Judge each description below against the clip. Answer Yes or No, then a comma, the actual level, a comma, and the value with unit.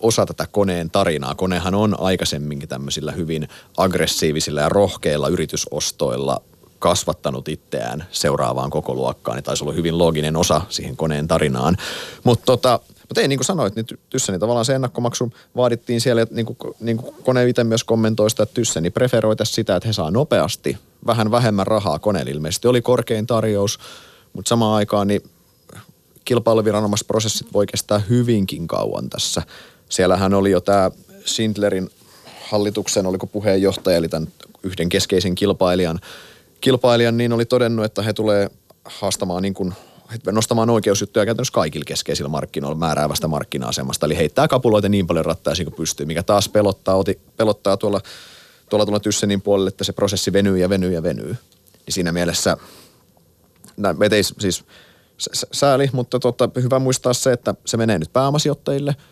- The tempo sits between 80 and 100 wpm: No, fast, 155 wpm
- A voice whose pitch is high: No, low, 105 Hz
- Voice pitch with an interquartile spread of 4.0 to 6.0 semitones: Yes, average, 4.5 semitones